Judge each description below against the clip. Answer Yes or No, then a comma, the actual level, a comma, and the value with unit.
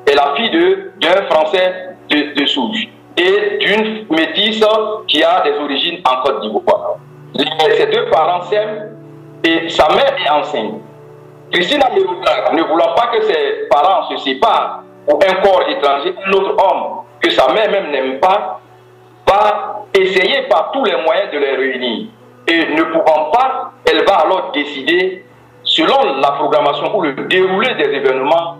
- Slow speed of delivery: No, average, 155 wpm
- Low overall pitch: No, high, 190 Hz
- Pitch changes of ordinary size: No, wide, 9.0 semitones